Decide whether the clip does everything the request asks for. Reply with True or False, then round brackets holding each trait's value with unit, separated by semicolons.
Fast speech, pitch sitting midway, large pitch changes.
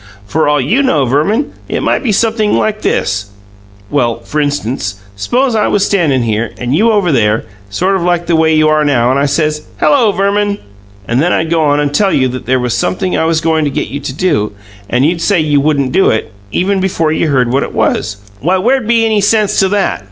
True (225 wpm; 155 Hz; 6.9 semitones)